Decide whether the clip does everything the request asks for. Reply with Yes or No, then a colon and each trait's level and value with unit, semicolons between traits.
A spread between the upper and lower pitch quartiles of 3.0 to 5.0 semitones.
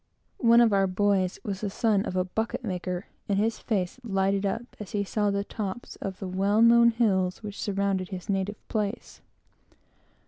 No: narrow, 2.4 semitones